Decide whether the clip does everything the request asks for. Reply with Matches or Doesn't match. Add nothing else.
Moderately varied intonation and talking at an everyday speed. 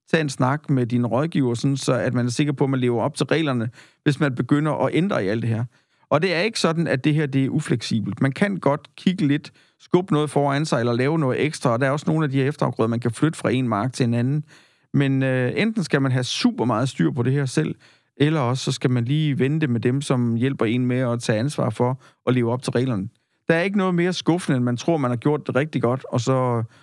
Doesn't match